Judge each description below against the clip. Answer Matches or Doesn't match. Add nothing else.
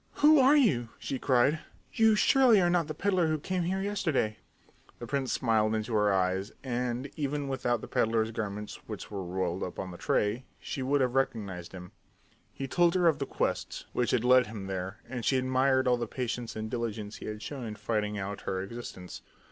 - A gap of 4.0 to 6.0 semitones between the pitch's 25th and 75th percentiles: Matches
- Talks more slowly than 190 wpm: Doesn't match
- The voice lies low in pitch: Matches